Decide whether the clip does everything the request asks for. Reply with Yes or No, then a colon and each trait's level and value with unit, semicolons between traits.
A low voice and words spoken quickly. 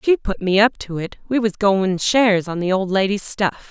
No: high, 200 Hz; fast, 245 wpm